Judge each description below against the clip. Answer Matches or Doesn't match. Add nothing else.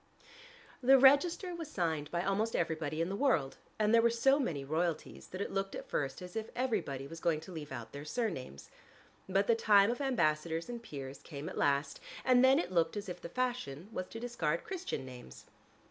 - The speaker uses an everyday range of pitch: Doesn't match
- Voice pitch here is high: Doesn't match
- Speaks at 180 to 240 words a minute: Matches